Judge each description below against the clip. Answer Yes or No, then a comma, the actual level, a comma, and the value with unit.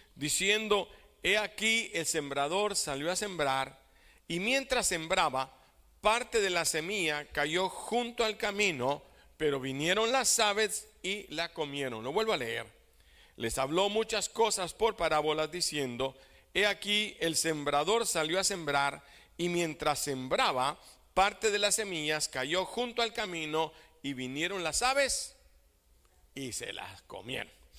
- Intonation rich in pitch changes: Yes, wide, 6.4 semitones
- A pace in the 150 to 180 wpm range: No, average, 135 wpm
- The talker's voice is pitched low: No, medium, 175 Hz